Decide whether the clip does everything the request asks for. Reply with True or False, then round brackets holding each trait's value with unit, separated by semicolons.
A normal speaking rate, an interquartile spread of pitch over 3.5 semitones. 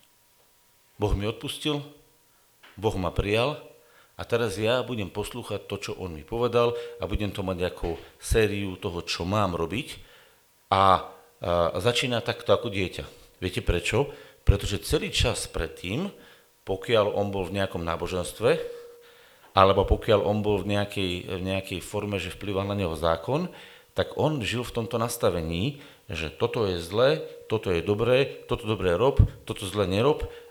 True (150 wpm; 5.1 semitones)